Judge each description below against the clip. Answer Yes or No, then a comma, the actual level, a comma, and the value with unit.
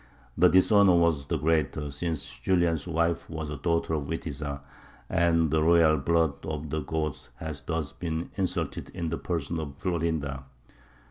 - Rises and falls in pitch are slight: Yes, narrow, 2.1 semitones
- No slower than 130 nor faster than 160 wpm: Yes, average, 155 wpm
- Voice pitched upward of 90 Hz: No, very low, 80 Hz